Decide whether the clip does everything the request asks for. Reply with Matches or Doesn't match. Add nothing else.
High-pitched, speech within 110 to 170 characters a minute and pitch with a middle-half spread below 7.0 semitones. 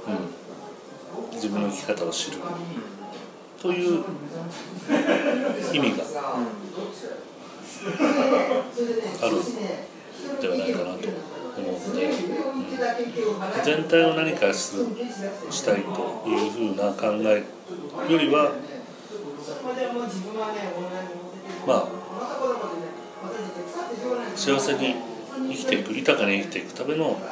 Doesn't match